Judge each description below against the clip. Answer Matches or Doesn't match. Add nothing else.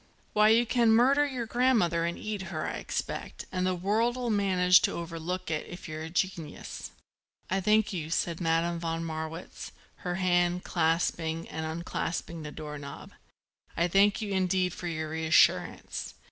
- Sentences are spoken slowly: Doesn't match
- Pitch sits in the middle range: Matches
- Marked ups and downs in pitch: Doesn't match